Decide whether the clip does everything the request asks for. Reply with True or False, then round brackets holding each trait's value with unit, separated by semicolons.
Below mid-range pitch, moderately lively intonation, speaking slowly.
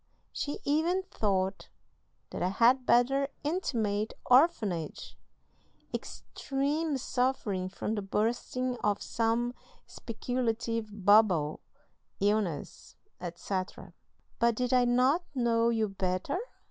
False (230 Hz; 4.0 semitones; 95 wpm)